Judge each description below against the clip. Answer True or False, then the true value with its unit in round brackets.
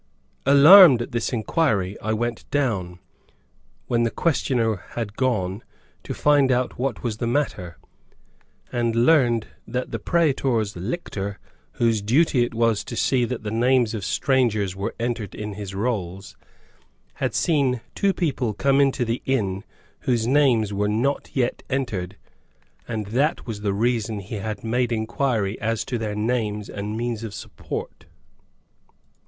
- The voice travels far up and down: False (3.5 semitones)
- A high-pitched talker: False (115 Hz)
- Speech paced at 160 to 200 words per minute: False (150 wpm)